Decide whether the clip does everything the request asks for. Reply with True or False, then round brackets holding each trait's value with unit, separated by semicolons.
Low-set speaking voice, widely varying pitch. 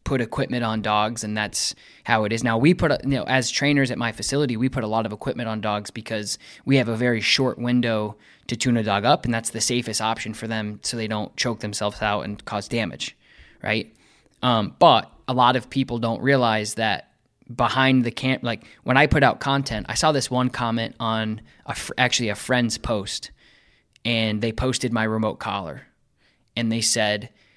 False (115 Hz; 2.6 semitones)